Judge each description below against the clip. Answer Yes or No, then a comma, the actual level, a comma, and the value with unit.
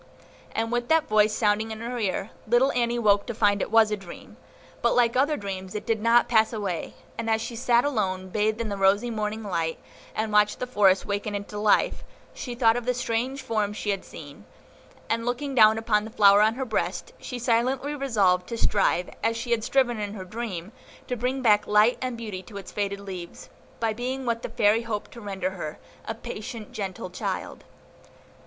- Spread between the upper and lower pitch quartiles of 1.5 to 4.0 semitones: Yes, average, 2.8 semitones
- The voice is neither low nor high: No, high, 220 Hz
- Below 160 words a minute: No, fast, 205 wpm